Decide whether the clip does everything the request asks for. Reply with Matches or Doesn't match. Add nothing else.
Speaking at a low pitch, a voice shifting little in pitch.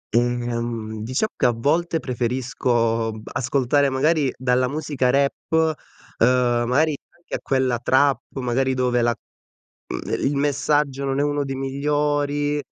Doesn't match